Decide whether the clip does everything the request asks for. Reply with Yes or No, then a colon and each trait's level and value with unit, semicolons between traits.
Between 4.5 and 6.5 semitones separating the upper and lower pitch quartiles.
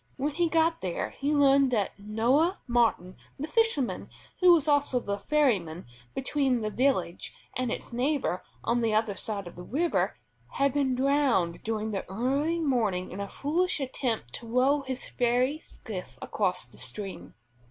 Yes: wide, 5.6 semitones